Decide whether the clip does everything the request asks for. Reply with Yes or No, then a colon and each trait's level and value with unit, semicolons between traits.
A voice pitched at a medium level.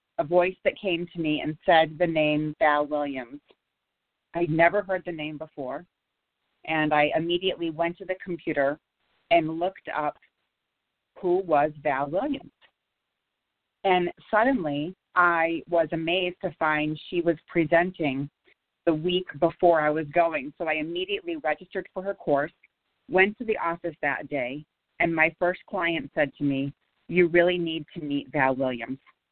Yes: medium, 170 Hz